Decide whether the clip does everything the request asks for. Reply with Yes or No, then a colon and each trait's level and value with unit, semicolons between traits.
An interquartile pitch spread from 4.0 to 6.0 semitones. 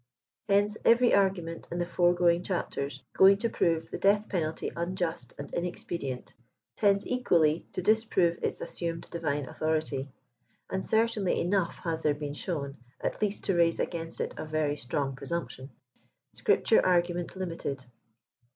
No: average, 3.6 semitones